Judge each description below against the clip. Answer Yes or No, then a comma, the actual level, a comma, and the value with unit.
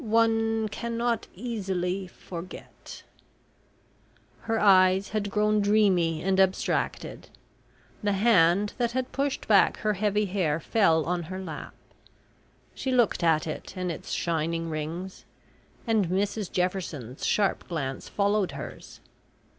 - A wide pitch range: No, average, 3.8 semitones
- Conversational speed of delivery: No, slow, 120 wpm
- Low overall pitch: No, high, 195 Hz